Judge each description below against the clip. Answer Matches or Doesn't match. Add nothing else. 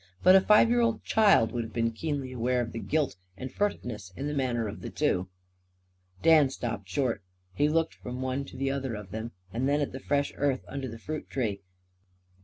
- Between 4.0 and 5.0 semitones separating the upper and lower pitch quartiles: Matches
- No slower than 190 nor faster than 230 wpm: Matches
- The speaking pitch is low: Matches